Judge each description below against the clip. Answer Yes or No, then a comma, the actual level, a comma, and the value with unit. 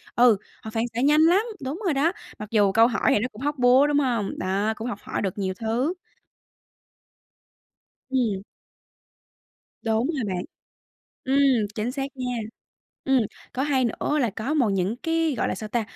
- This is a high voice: Yes, high, 245 Hz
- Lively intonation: No, average, 4.4 semitones